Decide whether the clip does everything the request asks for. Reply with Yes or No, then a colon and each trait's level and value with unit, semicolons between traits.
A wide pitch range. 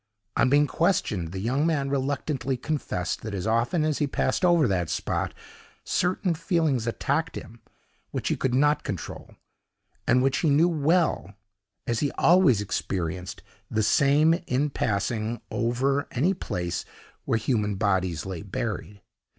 Yes: wide, 6.5 semitones